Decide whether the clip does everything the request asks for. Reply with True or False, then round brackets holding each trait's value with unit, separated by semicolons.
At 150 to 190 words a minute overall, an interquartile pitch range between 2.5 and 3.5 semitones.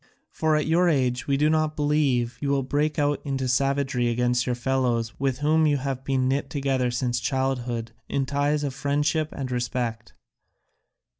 True (170 wpm; 2.9 semitones)